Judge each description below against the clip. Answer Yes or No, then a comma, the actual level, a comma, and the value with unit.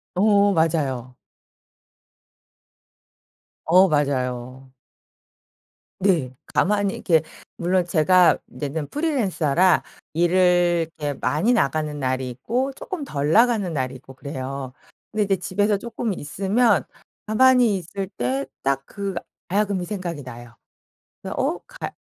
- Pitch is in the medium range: Yes, medium, 175 Hz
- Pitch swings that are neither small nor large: No, wide, 6.6 semitones